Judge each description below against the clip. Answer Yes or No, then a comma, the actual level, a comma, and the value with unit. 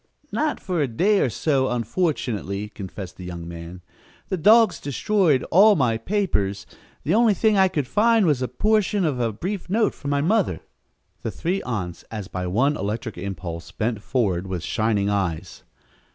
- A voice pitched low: Yes, low, 125 Hz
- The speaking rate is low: No, average, 170 wpm